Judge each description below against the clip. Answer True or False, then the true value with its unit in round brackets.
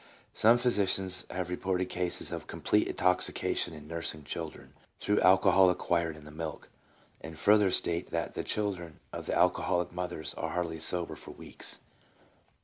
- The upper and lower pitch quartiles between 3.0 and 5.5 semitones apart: False (2.4 semitones)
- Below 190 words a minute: True (150 wpm)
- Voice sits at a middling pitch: False (90 Hz)